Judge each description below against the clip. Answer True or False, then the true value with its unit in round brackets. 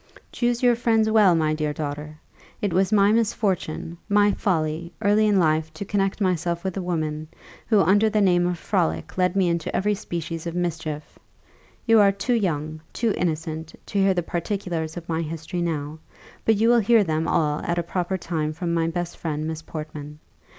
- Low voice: False (175 Hz)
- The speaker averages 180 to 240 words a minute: True (190 wpm)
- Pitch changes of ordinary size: True (4.2 semitones)